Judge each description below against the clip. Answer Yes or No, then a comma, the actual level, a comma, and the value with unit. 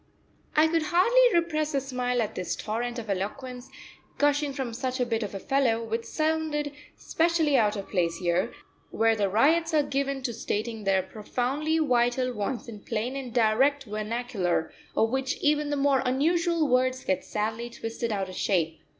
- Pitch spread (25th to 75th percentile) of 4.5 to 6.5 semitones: Yes, average, 5.0 semitones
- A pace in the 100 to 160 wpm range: No, average, 175 wpm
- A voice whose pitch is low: No, very high, 250 Hz